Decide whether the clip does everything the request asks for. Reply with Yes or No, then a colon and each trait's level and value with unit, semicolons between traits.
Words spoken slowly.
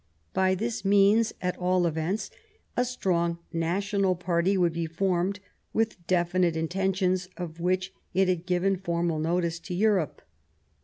No: average, 145 wpm